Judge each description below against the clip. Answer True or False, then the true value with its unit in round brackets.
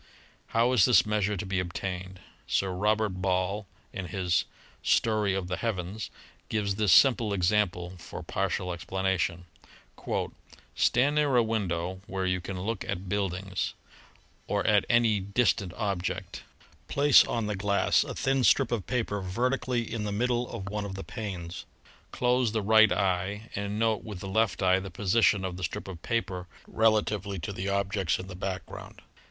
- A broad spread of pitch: False (3.1 semitones)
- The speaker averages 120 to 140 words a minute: False (165 wpm)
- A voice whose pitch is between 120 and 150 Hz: False (100 Hz)